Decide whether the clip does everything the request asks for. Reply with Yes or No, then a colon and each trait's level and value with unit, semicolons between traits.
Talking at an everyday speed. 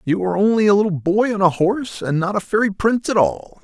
No: fast, 265 wpm